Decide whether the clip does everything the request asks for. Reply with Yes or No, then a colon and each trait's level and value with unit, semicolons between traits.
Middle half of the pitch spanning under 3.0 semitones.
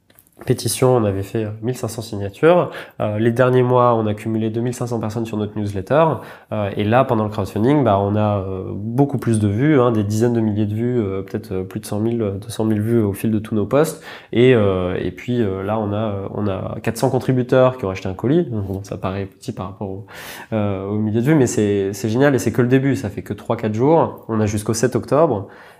No: average, 3.3 semitones